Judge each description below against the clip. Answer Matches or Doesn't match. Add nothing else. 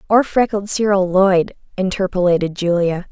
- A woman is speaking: Matches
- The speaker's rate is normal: Doesn't match